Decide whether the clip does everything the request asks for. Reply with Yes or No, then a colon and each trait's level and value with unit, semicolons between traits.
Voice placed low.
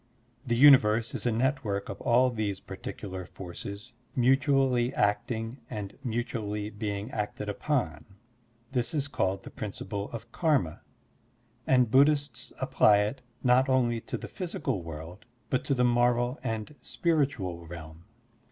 Yes: low, 115 Hz